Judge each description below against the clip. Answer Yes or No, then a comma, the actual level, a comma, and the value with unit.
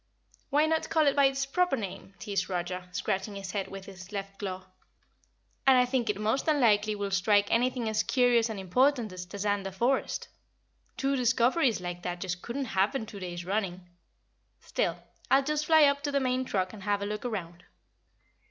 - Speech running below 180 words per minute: No, average, 185 wpm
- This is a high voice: Yes, high, 210 Hz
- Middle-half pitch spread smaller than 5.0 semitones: No, wide, 5.4 semitones